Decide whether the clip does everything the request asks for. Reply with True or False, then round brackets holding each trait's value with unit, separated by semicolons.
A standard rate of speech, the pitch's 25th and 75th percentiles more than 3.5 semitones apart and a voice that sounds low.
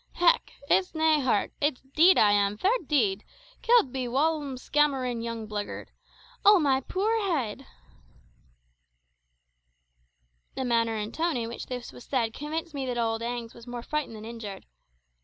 False (155 wpm; 5.0 semitones; 255 Hz)